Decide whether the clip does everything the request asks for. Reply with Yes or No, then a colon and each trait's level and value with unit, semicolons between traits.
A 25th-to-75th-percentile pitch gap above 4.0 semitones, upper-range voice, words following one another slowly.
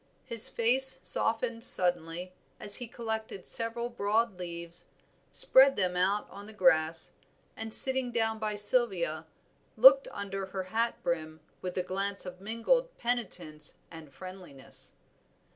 Yes: average, 4.5 semitones; high, 200 Hz; slow, 125 wpm